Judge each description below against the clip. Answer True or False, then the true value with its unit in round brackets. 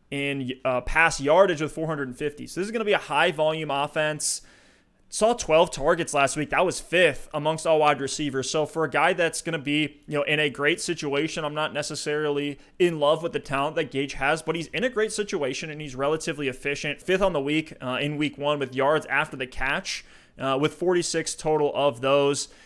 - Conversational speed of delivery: False (215 wpm)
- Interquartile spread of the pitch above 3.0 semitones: False (2.4 semitones)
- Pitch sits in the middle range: True (150 Hz)